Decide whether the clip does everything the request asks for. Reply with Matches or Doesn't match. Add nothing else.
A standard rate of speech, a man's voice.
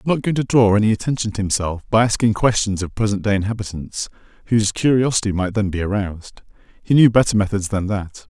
Doesn't match